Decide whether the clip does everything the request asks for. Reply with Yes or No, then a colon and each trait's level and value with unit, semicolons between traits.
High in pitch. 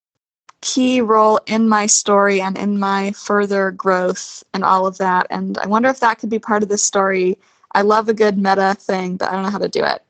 Yes: high, 200 Hz